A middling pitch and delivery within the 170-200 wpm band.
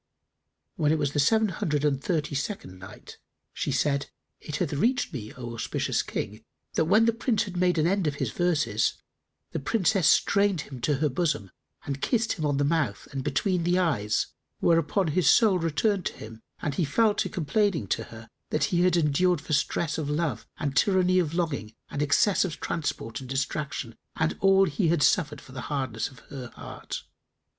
Yes: medium, 155 Hz; average, 195 wpm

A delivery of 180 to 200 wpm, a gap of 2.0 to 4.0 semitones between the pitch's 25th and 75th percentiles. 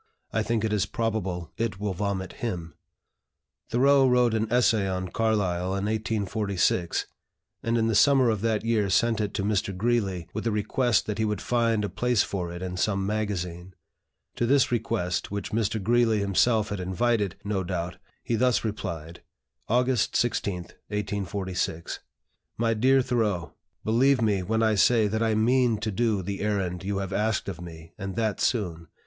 No: average, 170 wpm; average, 3.2 semitones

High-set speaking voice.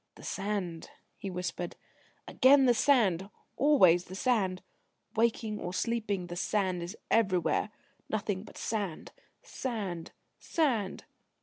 Yes: high, 200 Hz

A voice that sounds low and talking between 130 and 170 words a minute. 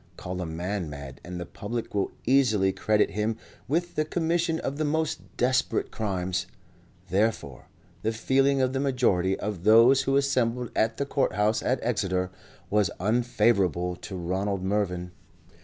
Yes: low, 105 Hz; average, 155 wpm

